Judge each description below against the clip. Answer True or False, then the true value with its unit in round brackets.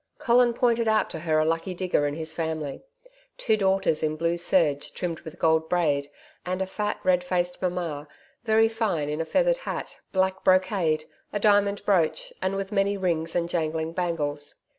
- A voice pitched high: False (175 Hz)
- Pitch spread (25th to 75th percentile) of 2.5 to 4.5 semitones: True (3.7 semitones)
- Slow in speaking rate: False (180 wpm)